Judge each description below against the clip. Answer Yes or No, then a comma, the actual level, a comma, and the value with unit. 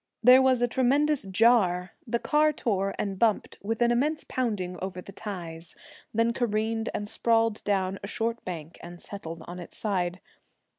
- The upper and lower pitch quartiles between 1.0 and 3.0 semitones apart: No, average, 4.4 semitones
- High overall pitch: Yes, high, 210 Hz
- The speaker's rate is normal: Yes, average, 165 wpm